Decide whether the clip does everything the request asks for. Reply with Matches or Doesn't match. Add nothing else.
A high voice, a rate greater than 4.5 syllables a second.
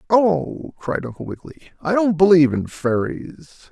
Doesn't match